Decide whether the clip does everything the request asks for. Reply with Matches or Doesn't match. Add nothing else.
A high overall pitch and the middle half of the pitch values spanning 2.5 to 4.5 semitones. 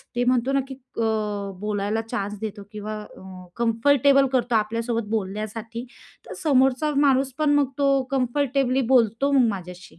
Matches